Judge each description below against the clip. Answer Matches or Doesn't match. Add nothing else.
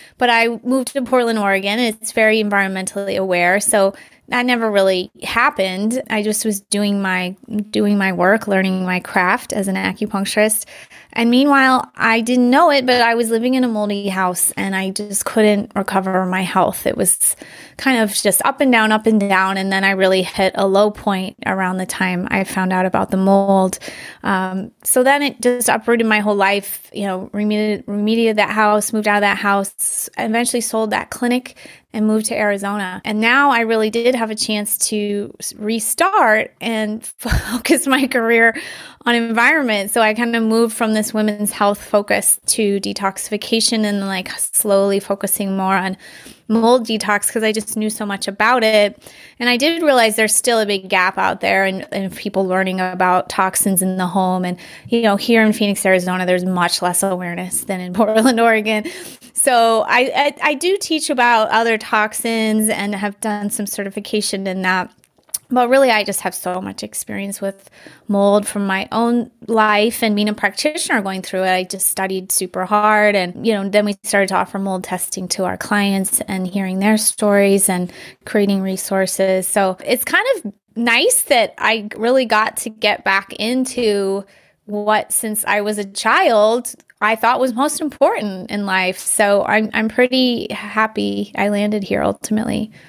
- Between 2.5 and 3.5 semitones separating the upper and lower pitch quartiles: Matches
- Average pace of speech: Matches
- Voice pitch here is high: Matches